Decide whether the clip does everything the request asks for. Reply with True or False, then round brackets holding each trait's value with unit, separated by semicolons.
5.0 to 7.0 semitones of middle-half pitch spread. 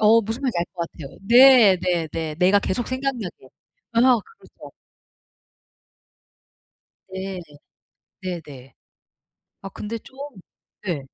True (5.6 semitones)